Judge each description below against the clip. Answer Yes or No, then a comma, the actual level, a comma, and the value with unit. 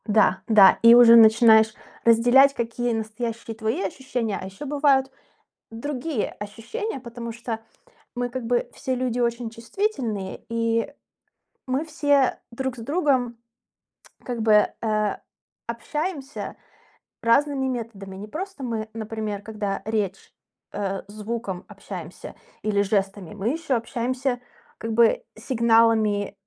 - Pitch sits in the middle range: No, high, 230 Hz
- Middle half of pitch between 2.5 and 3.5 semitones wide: Yes, average, 3.1 semitones